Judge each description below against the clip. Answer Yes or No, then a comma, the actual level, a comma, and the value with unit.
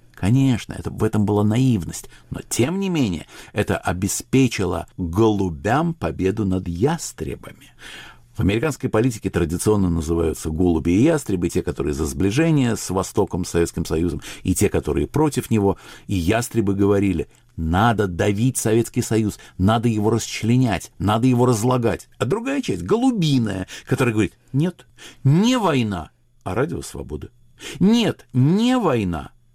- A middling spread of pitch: No, wide, 5.9 semitones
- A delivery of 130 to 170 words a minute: Yes, average, 135 wpm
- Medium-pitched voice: No, low, 110 Hz